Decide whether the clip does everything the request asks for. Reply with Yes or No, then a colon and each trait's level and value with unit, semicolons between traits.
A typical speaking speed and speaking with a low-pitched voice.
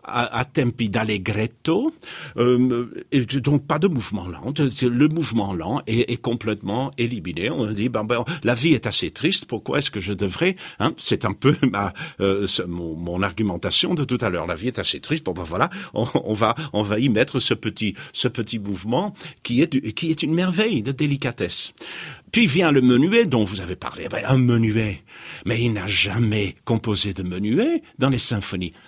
Yes: average, 200 wpm; low, 120 Hz